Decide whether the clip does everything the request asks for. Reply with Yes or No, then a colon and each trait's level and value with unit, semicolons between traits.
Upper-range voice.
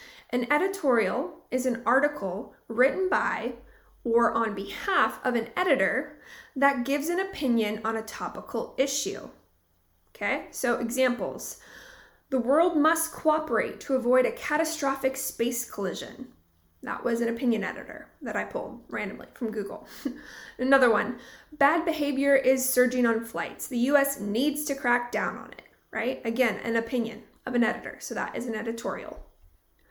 Yes: very high, 255 Hz